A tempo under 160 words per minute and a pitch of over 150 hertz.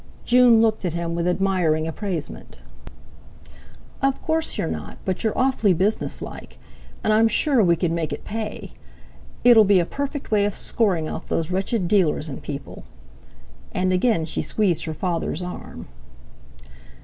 Yes: average, 150 wpm; high, 190 Hz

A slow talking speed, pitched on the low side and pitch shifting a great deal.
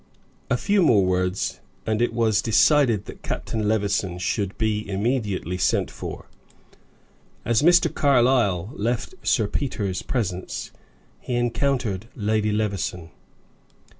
No: slow, 115 wpm; low, 110 Hz; average, 3.7 semitones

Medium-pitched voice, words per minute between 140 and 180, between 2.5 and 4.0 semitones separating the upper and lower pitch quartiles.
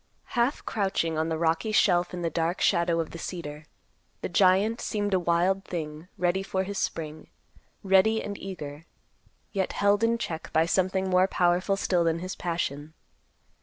Yes: medium, 180 Hz; average, 165 wpm; average, 2.8 semitones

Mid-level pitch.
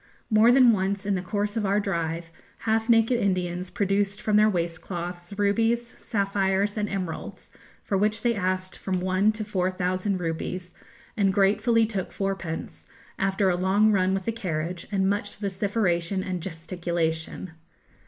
No: high, 195 Hz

